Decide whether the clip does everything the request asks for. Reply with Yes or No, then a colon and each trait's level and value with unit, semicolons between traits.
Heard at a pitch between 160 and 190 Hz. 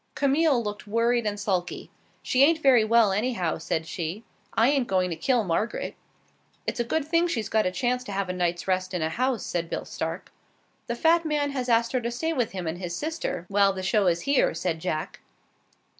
No: high, 220 Hz